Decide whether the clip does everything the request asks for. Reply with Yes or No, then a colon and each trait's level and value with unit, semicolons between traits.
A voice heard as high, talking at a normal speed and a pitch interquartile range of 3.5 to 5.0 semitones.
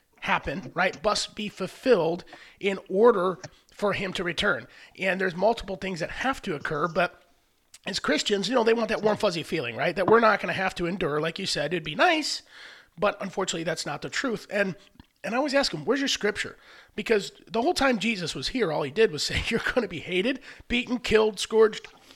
No: high, 205 Hz; fast, 215 wpm; average, 3.9 semitones